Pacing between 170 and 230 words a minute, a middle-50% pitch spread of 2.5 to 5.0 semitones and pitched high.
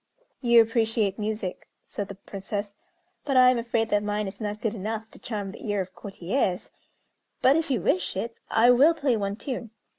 Yes: average, 190 wpm; average, 2.9 semitones; high, 215 Hz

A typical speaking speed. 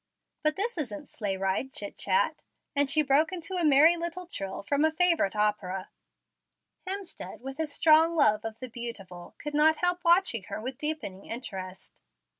Yes: average, 170 wpm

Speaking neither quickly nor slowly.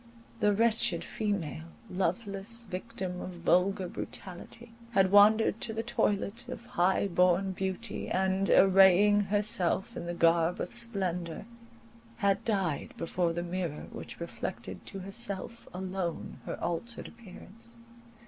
No: slow, 125 wpm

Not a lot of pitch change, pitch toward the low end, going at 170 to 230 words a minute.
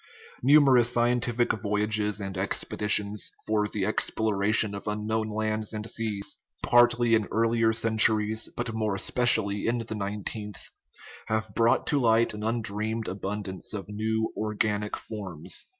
No: narrow, 1.5 semitones; low, 110 Hz; slow, 135 wpm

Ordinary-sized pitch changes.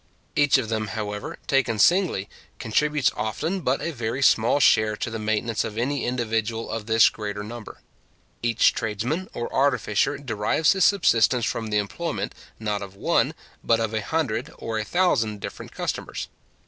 Yes: average, 4.0 semitones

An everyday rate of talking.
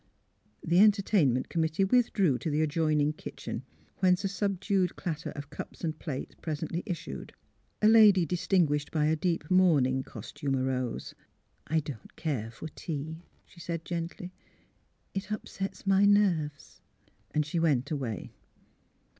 Yes: average, 145 wpm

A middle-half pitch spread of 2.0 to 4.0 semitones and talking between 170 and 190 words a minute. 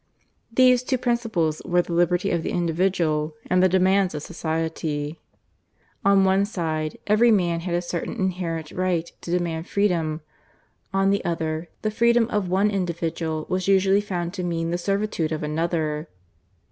No: average, 3.1 semitones; average, 160 wpm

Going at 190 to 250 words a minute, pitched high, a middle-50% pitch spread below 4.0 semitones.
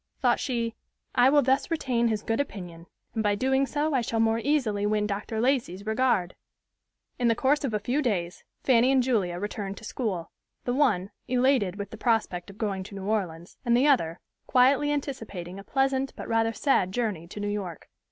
No: average, 195 wpm; high, 225 Hz; average, 4.8 semitones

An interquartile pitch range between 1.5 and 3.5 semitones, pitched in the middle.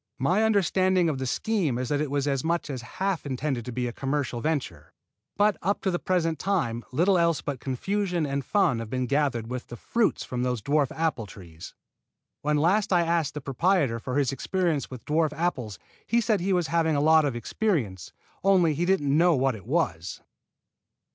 No: wide, 5.6 semitones; medium, 150 Hz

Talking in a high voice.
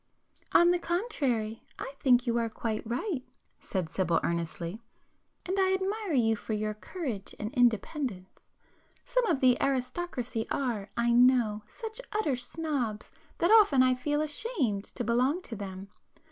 Yes: very high, 250 Hz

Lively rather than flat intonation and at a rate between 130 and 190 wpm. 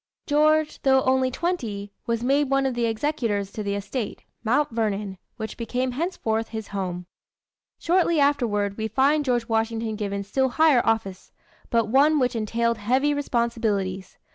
No: average, 4.3 semitones; average, 150 wpm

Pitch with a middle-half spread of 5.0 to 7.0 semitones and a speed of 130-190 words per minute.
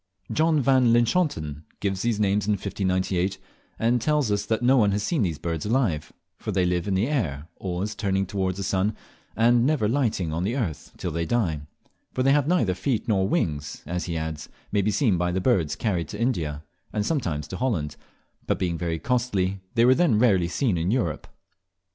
No: wide, 5.4 semitones; average, 200 wpm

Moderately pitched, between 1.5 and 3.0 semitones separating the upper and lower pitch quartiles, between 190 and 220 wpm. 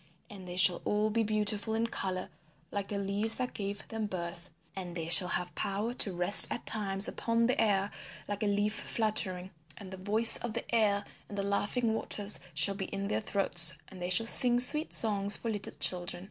No: high, 200 Hz; narrow, 2.6 semitones; average, 200 wpm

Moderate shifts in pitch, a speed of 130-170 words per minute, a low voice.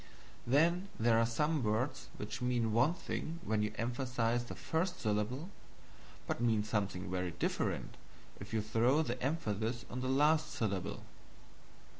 Yes: average, 4.8 semitones; average, 145 wpm; low, 120 Hz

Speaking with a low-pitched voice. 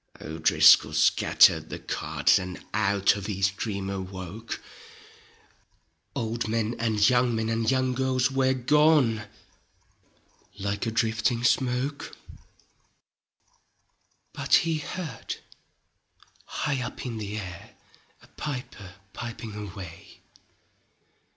Yes: low, 115 Hz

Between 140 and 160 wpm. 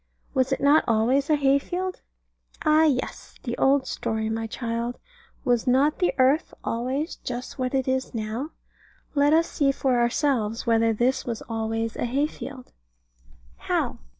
Yes: average, 155 wpm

